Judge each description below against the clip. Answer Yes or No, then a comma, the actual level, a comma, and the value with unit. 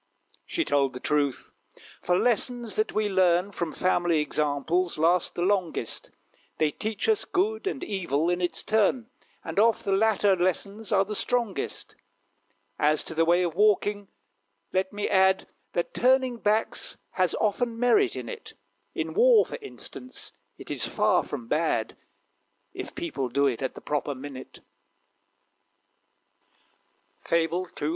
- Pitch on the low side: No, high, 190 Hz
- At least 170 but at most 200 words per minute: No, average, 145 wpm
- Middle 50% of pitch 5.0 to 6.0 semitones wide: Yes, wide, 5.5 semitones